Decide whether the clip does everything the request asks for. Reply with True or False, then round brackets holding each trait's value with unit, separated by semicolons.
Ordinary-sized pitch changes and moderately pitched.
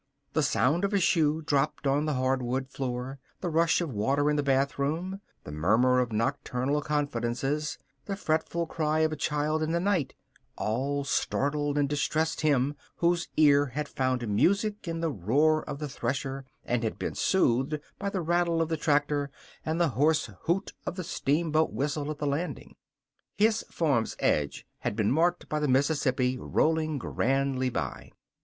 True (3.3 semitones; 145 Hz)